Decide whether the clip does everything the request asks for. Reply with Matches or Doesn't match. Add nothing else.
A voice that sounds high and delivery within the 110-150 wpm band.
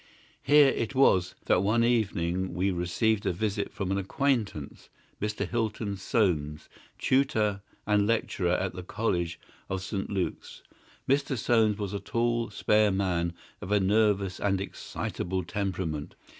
Doesn't match